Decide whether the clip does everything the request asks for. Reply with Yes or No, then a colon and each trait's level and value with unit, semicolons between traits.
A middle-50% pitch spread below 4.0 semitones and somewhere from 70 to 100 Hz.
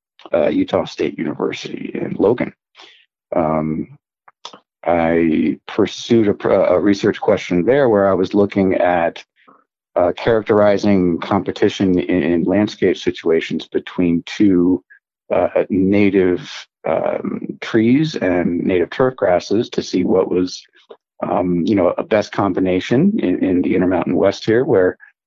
Yes: narrow, 2.5 semitones; very low, 95 Hz